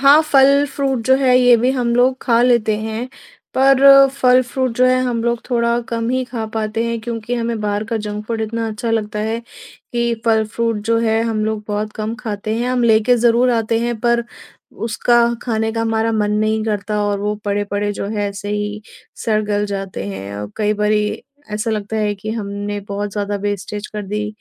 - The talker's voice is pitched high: Yes, high, 220 Hz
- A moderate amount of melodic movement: No, narrow, 2.3 semitones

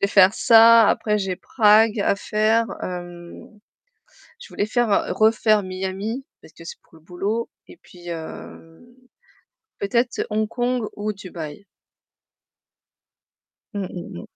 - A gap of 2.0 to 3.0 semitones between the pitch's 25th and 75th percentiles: No, average, 3.4 semitones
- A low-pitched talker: No, high, 210 Hz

